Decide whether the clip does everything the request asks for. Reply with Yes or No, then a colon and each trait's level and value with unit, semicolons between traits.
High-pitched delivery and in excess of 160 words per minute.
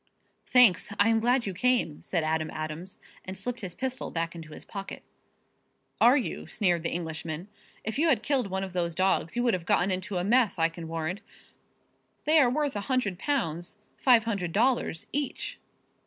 Yes: high, 195 Hz; average, 185 wpm